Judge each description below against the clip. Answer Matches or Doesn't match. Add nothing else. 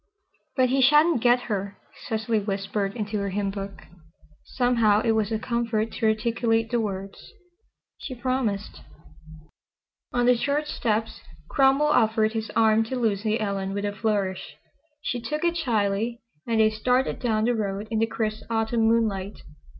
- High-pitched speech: Matches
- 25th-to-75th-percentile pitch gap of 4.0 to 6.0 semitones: Doesn't match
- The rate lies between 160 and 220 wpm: Doesn't match